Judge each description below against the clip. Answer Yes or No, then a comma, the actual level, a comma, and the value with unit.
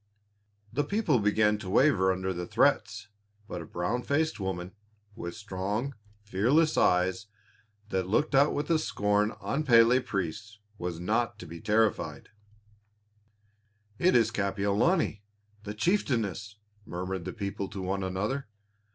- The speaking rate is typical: No, slow, 130 wpm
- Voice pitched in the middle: No, low, 105 Hz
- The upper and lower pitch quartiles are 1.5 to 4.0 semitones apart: No, average, 4.7 semitones